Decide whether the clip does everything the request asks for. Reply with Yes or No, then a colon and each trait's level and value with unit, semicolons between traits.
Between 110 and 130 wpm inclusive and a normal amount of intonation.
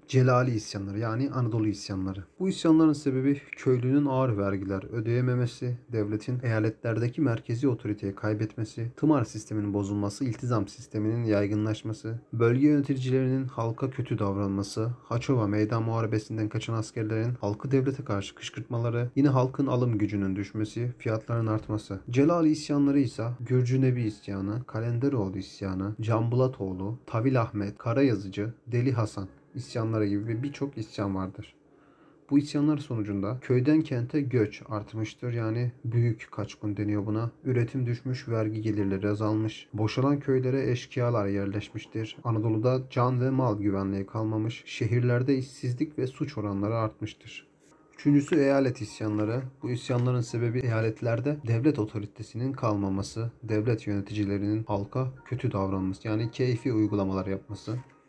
Yes: average, 120 wpm; average, 3.5 semitones